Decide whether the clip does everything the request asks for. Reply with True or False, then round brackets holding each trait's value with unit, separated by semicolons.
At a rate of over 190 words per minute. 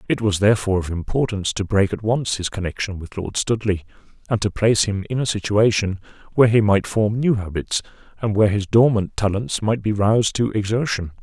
True (200 wpm)